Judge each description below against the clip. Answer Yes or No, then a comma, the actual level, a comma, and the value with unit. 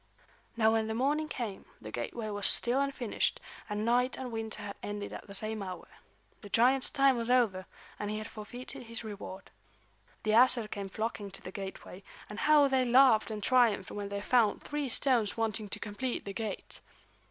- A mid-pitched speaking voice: No, high, 220 Hz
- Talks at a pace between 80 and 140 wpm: No, average, 185 wpm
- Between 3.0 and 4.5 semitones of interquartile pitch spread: Yes, average, 3.5 semitones